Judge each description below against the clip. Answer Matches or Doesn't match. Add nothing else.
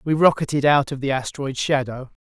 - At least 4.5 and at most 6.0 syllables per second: Matches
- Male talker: Matches